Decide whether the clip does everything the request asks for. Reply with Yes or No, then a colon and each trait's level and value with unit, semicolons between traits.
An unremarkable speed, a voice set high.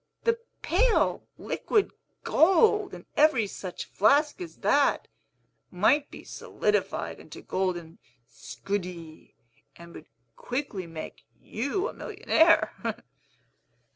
No: slow, 100 wpm; very high, 270 Hz